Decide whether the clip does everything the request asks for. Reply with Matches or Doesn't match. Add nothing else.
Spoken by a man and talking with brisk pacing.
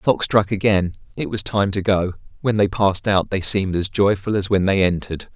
Matches